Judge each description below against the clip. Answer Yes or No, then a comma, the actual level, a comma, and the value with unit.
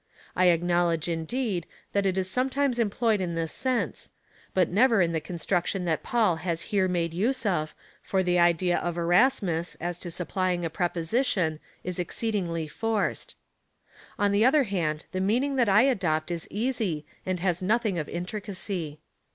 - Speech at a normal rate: Yes, average, 160 wpm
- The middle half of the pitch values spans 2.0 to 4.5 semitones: Yes, average, 4.0 semitones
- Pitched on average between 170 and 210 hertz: Yes, medium, 185 Hz